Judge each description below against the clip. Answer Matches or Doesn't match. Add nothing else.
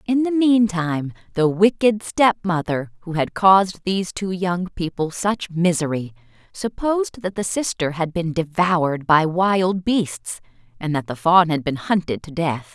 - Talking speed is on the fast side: Doesn't match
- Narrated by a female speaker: Matches